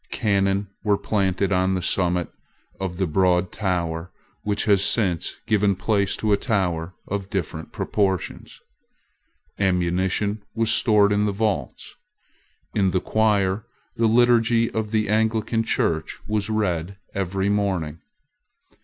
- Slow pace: Yes, slow, 125 wpm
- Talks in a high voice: No, low, 100 Hz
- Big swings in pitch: No, narrow, 2.6 semitones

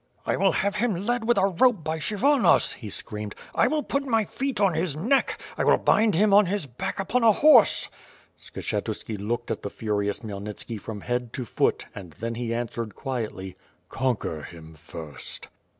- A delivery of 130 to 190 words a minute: Yes, average, 180 wpm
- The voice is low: Yes, low, 130 Hz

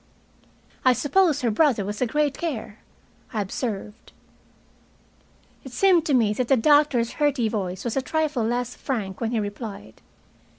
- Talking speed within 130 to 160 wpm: Yes, average, 155 wpm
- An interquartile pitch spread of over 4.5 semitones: Yes, average, 5.2 semitones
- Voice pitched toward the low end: No, high, 245 Hz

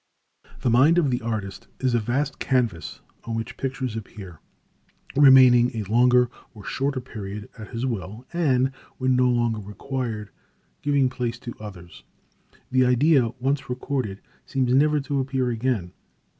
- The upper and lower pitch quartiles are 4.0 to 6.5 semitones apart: No, average, 2.9 semitones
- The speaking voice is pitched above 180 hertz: No, low, 125 Hz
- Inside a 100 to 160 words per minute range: Yes, average, 145 wpm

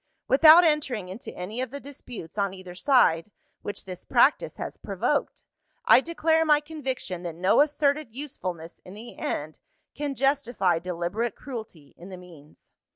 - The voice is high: Yes, high, 225 Hz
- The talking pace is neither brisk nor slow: Yes, average, 155 wpm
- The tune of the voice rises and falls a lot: Yes, wide, 7.9 semitones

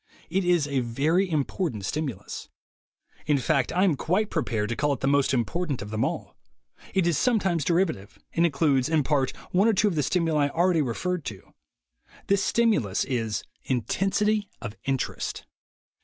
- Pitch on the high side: No, medium, 150 Hz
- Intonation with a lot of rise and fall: Yes, wide, 5.8 semitones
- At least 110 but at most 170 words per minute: Yes, average, 165 wpm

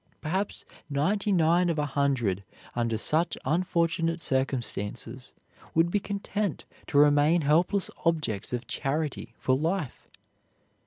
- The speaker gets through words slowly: Yes, slow, 115 wpm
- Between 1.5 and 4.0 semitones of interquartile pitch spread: No, average, 4.6 semitones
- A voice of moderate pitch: Yes, medium, 155 Hz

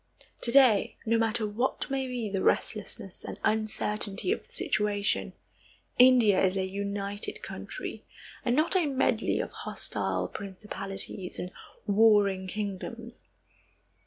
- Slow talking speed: Yes, slow, 125 wpm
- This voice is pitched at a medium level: No, high, 210 Hz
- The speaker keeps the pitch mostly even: No, average, 3.3 semitones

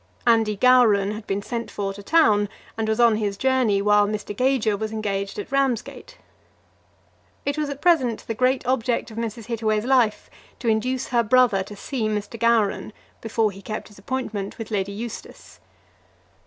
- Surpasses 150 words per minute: Yes, average, 170 wpm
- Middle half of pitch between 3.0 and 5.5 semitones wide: Yes, average, 3.3 semitones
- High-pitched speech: Yes, high, 220 Hz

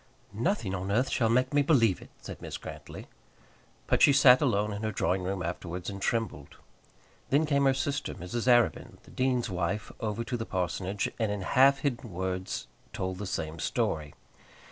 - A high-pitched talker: No, low, 105 Hz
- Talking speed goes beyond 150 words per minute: Yes, average, 180 wpm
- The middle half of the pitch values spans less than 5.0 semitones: No, wide, 5.6 semitones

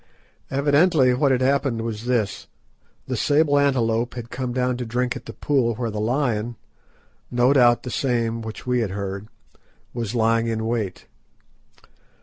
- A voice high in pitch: No, low, 120 Hz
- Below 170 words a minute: Yes, average, 145 wpm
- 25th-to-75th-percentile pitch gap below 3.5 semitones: Yes, narrow, 2.4 semitones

